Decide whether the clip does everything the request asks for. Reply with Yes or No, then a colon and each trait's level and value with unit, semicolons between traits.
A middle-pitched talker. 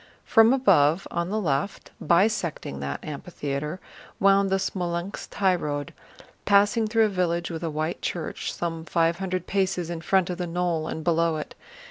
Yes: medium, 175 Hz